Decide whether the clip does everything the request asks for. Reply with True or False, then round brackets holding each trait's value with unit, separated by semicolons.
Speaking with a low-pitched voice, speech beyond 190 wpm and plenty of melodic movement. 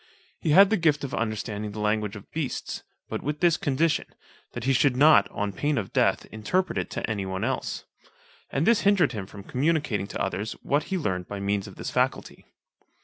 True (125 Hz; 200 wpm; 7.0 semitones)